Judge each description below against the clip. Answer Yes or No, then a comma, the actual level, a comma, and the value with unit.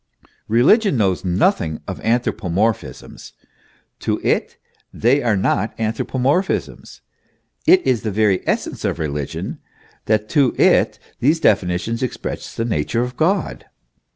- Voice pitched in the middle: No, low, 115 Hz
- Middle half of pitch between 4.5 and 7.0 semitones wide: Yes, average, 5.2 semitones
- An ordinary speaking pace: No, slow, 125 wpm